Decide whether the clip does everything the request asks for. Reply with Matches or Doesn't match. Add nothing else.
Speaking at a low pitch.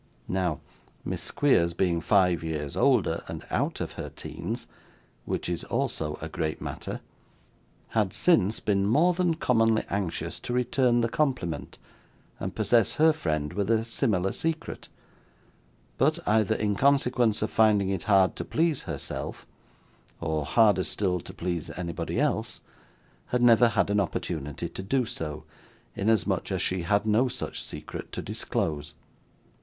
Matches